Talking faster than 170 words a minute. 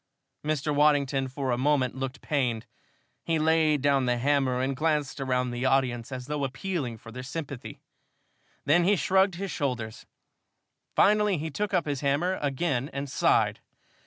No: average, 160 wpm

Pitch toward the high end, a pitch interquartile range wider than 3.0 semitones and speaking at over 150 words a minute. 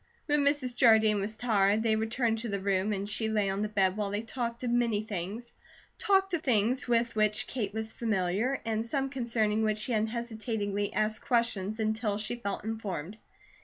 No: high, 220 Hz; narrow, 2.4 semitones; average, 185 wpm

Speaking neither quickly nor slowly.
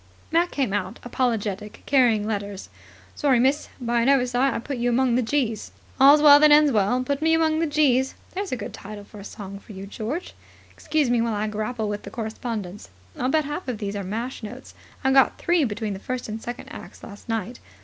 No: fast, 215 wpm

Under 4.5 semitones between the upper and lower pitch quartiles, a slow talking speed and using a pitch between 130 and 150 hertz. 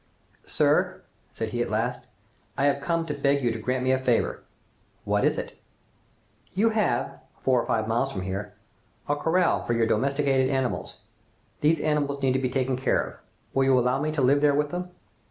No: average, 2.9 semitones; average, 195 wpm; low, 135 Hz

